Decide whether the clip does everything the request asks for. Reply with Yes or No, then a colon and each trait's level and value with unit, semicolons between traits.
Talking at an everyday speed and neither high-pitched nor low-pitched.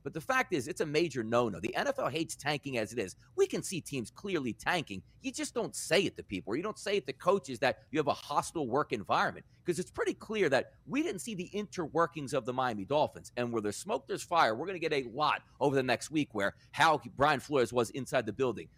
No: fast, 255 wpm; medium, 145 Hz